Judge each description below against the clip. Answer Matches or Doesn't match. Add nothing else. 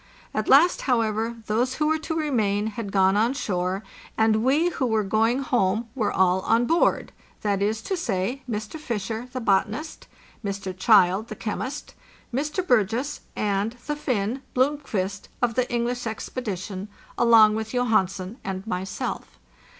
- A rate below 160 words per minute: Matches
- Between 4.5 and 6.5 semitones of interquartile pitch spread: Doesn't match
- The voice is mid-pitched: Doesn't match